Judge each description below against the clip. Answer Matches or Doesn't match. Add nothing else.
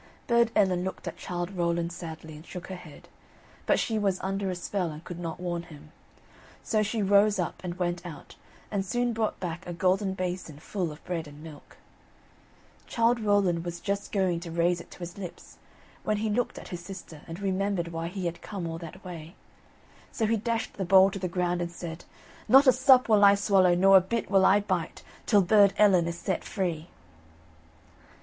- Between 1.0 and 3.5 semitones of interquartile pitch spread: Matches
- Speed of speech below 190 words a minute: Doesn't match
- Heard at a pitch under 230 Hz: Matches